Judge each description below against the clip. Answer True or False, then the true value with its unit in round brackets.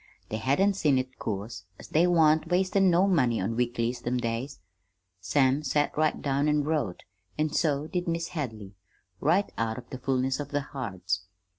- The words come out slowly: False (175 wpm)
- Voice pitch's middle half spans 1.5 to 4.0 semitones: False (5.1 semitones)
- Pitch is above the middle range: False (140 Hz)